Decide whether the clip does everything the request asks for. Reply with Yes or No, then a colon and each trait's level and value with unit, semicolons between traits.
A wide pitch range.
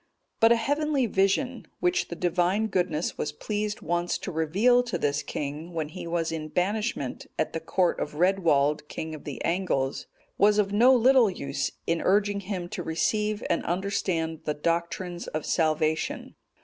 No: average, 4.7 semitones